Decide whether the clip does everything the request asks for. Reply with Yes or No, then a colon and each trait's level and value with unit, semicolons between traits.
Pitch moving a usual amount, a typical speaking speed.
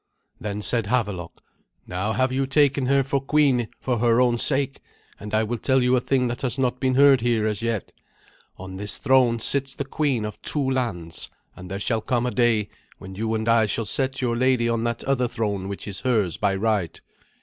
No: average, 3.6 semitones; fast, 210 wpm